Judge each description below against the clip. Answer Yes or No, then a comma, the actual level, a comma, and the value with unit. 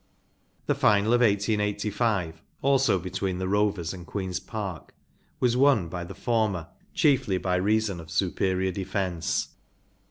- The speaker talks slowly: Yes, slow, 130 wpm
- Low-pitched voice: Yes, low, 100 Hz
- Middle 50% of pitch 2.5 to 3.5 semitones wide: Yes, average, 3.1 semitones